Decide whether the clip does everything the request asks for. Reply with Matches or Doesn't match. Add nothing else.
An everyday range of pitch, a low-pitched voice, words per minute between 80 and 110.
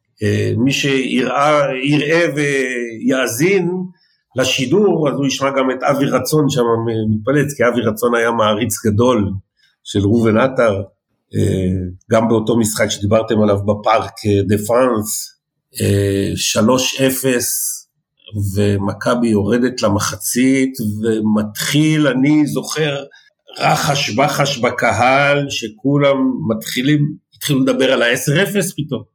Matches